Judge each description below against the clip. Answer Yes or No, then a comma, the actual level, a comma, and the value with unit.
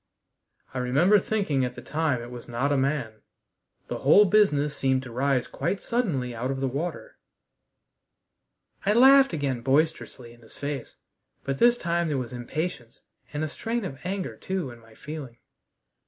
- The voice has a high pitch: No, medium, 140 Hz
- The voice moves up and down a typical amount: No, wide, 6.0 semitones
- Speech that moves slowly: No, average, 170 wpm